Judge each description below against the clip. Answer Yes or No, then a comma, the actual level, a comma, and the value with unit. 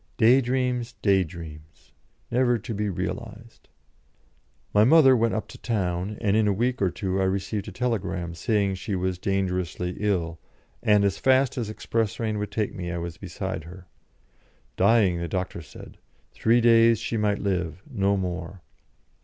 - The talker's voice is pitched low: Yes, low, 100 Hz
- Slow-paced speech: No, average, 165 wpm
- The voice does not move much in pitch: No, average, 3.9 semitones